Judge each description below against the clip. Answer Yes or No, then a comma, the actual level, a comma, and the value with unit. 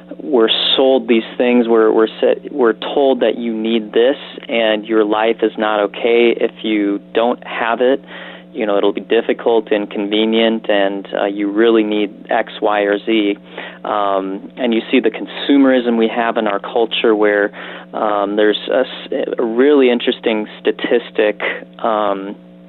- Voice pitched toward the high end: No, low, 110 Hz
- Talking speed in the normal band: Yes, average, 160 wpm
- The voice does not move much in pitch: Yes, narrow, 2.1 semitones